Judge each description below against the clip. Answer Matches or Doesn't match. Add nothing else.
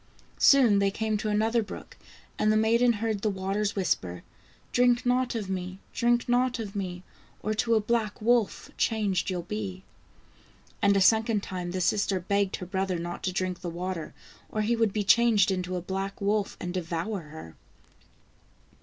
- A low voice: Doesn't match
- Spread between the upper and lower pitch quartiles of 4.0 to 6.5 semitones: Doesn't match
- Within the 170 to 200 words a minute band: Matches